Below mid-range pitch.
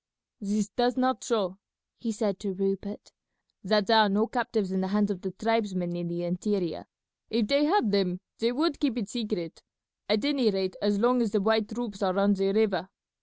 No: high, 205 Hz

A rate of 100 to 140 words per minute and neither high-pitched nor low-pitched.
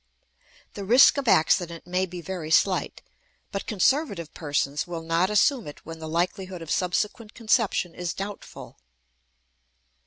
Yes: slow, 135 wpm; medium, 180 Hz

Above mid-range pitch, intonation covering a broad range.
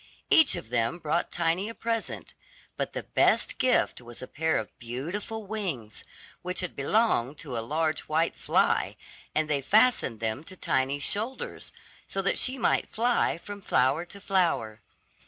No: medium, 165 Hz; wide, 7.8 semitones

